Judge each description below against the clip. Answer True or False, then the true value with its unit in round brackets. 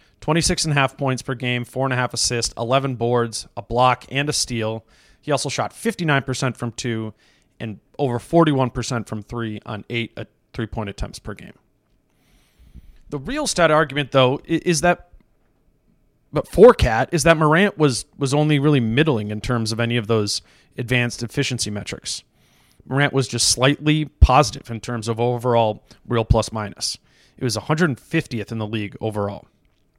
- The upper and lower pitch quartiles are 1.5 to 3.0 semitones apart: False (4.0 semitones)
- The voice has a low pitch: True (125 Hz)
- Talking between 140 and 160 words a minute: False (170 wpm)